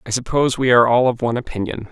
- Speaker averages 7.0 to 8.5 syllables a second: Yes, 7.8 syllables/s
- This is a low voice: Yes, low, 120 Hz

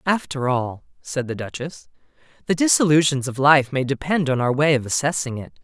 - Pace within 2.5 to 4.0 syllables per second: No, 5.4 syllables/s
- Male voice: Yes, male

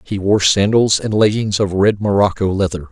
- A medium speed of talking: Yes, average, 185 wpm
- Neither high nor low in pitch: No, low, 100 Hz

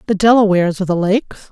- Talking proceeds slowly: No, average, 200 wpm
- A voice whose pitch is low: No, high, 200 Hz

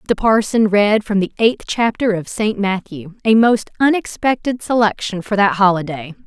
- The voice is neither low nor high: No, high, 210 Hz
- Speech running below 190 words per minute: Yes, average, 165 wpm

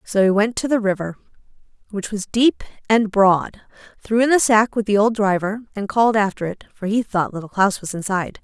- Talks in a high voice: Yes, high, 210 Hz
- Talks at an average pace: No, fast, 215 wpm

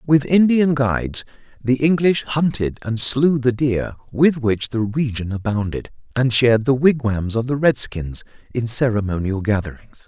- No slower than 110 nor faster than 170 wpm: Yes, average, 150 wpm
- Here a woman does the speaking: No, male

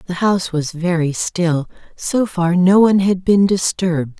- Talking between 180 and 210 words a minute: No, average, 170 wpm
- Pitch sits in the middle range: Yes, medium, 180 Hz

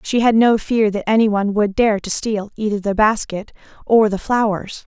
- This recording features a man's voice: No, female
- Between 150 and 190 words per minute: No, fast, 205 wpm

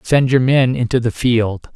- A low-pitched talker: Yes, low, 125 Hz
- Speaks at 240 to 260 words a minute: No, fast, 205 wpm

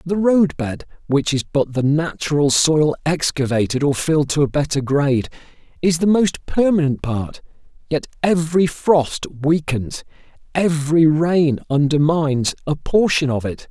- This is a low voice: No, medium, 150 Hz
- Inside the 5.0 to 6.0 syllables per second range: No, 4.5 syllables/s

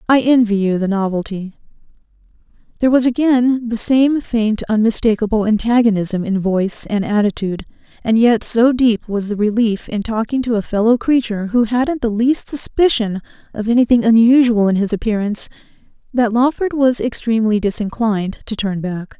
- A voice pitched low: No, high, 225 Hz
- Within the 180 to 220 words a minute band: No, average, 155 wpm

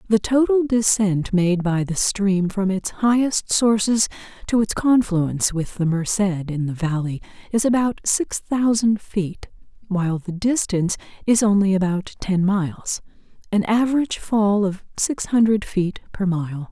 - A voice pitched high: Yes, high, 200 Hz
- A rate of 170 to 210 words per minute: No, average, 150 wpm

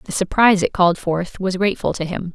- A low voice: No, medium, 185 Hz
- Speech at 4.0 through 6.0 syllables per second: No, 6.3 syllables/s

